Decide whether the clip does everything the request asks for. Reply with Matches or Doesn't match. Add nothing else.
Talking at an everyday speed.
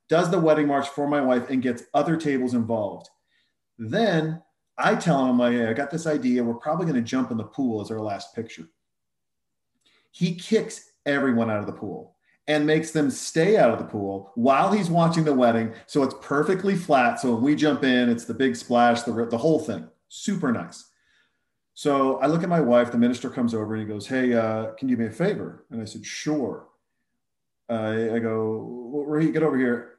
Doesn't match